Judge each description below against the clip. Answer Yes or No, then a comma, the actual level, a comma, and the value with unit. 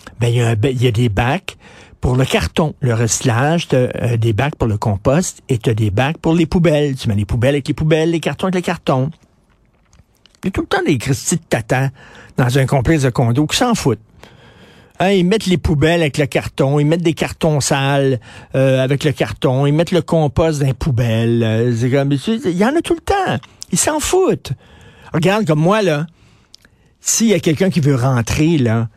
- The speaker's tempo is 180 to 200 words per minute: No, average, 215 wpm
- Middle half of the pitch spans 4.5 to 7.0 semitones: Yes, average, 5.3 semitones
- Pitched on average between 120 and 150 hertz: Yes, medium, 140 Hz